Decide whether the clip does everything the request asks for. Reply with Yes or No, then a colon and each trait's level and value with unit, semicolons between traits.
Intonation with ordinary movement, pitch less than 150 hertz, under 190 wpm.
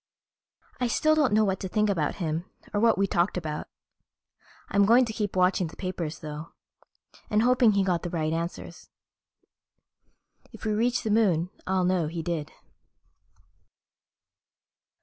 No: average, 4.2 semitones; medium, 185 Hz; average, 150 wpm